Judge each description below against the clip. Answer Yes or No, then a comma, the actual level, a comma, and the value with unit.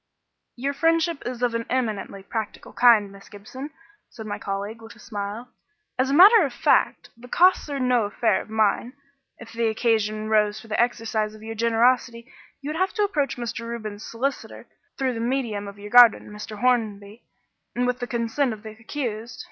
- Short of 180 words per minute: No, average, 190 wpm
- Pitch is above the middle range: Yes, high, 230 Hz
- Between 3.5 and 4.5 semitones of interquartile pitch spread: No, average, 2.7 semitones